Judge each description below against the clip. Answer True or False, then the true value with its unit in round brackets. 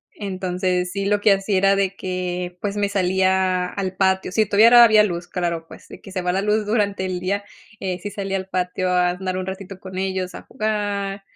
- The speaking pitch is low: False (190 Hz)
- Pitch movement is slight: True (1.6 semitones)